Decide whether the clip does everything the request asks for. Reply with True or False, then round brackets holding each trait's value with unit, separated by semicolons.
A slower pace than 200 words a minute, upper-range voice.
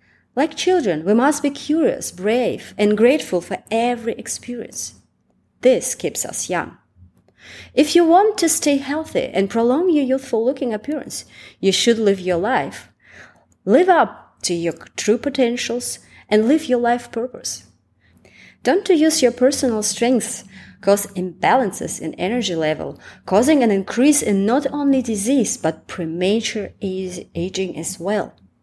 True (145 wpm; 235 Hz)